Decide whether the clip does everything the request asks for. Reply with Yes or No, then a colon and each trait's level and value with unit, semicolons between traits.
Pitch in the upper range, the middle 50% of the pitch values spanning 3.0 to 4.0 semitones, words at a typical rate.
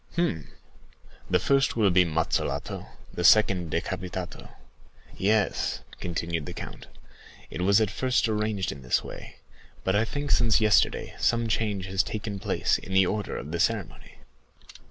No: low, 100 Hz; average, 3.6 semitones; average, 150 wpm